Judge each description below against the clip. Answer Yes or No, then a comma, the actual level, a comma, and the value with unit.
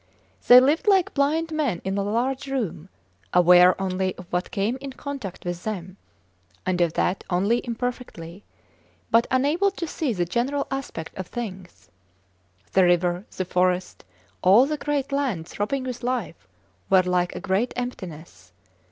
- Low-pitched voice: No, high, 205 Hz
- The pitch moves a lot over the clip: Yes, wide, 6.8 semitones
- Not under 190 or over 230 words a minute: No, average, 150 wpm